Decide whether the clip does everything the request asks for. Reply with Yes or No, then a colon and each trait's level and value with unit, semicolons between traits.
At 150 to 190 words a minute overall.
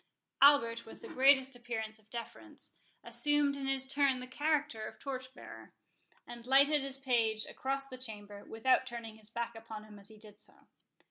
Yes: average, 180 wpm